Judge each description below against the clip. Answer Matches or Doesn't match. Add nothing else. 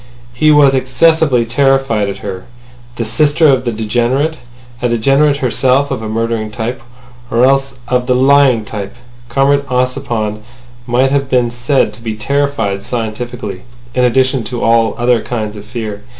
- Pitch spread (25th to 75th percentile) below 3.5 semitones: Matches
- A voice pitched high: Doesn't match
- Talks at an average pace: Matches